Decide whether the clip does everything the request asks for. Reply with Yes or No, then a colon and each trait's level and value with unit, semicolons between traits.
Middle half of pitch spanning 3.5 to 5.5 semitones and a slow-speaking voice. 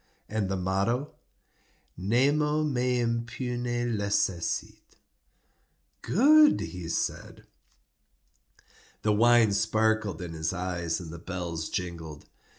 Yes: average, 5.1 semitones; slow, 95 wpm